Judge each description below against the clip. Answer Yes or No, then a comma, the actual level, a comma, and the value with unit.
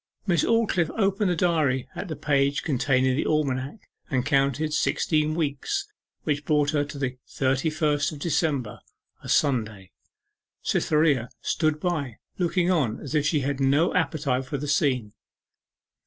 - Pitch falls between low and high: Yes, medium, 145 Hz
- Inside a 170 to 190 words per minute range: No, average, 150 wpm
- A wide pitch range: No, average, 3.0 semitones